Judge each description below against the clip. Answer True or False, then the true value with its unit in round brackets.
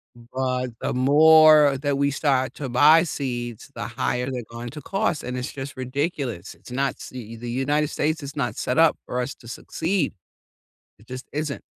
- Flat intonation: False (3.2 semitones)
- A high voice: False (135 Hz)